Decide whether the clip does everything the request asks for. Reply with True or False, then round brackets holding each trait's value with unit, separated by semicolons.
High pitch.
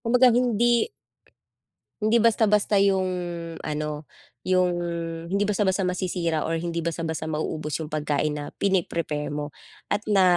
False (180 Hz)